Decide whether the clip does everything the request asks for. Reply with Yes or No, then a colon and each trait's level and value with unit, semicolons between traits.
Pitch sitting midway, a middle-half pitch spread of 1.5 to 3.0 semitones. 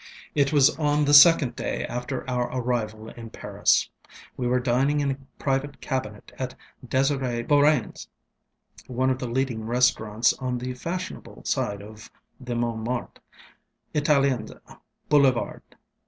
No: low, 130 Hz; average, 2.7 semitones